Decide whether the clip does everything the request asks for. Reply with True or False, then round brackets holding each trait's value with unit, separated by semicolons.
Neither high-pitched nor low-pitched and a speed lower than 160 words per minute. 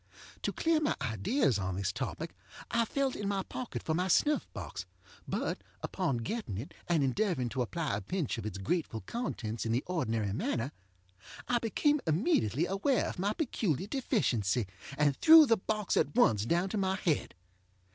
False (175 Hz; 175 wpm)